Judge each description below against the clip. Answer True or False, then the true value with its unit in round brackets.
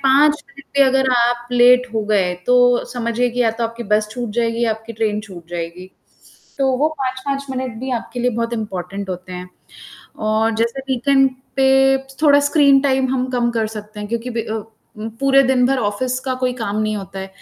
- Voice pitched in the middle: False (240 Hz)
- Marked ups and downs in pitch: False (3.4 semitones)